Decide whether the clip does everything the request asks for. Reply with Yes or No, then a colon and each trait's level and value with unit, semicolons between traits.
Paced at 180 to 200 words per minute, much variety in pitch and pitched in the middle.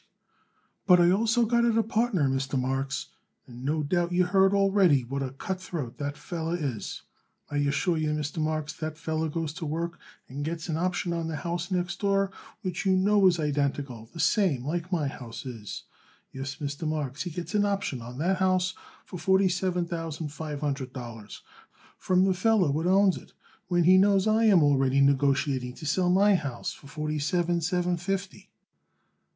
No: average, 185 wpm; average, 4.6 semitones; medium, 165 Hz